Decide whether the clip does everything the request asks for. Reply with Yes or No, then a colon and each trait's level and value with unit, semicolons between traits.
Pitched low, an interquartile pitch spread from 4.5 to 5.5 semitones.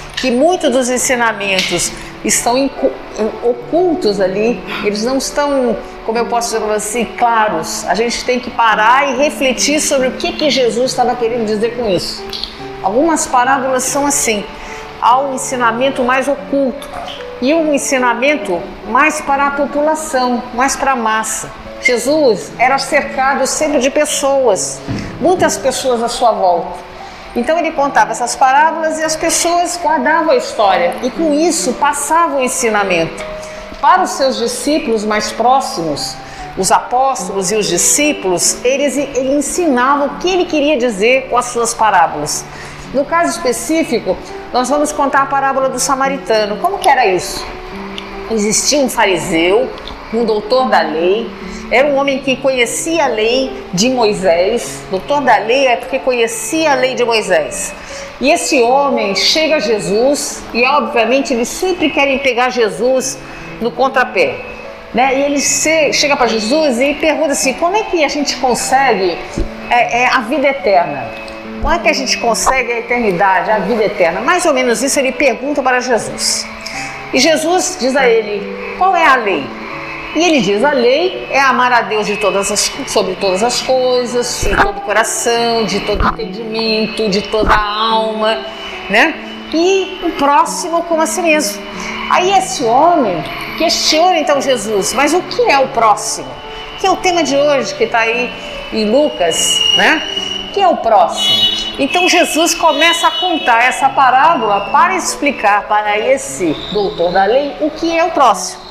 No: very high, 260 Hz; average, 4.8 semitones